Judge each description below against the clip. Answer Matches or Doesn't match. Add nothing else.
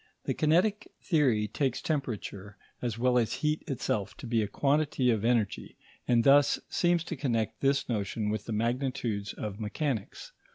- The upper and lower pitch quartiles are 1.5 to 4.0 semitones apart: Doesn't match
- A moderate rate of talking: Matches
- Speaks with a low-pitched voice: Matches